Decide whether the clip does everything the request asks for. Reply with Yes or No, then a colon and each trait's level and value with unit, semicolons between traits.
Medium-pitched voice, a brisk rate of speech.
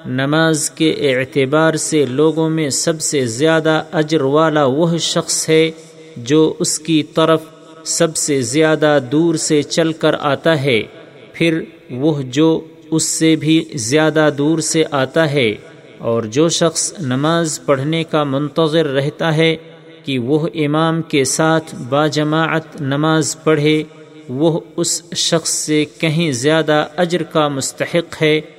No: medium, 155 Hz; average, 140 wpm